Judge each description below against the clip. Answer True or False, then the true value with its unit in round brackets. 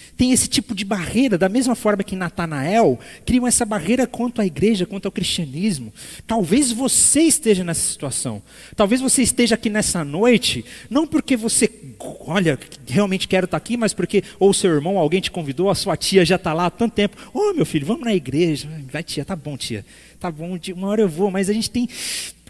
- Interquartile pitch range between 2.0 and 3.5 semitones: False (5.0 semitones)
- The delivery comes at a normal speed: False (210 wpm)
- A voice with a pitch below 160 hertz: False (195 Hz)